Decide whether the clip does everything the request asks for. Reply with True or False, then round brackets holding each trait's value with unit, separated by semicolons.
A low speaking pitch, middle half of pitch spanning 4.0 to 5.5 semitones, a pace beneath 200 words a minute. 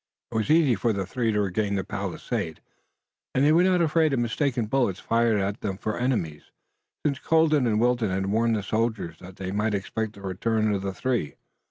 False (110 Hz; 4.5 semitones; 205 wpm)